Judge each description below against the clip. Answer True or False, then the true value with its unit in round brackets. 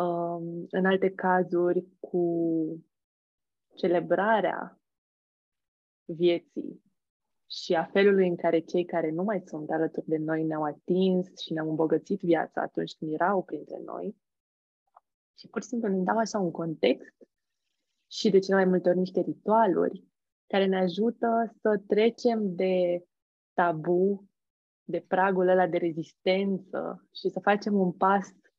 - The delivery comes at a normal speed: True (135 wpm)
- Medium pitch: True (180 Hz)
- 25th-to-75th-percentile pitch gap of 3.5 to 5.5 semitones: False (2.6 semitones)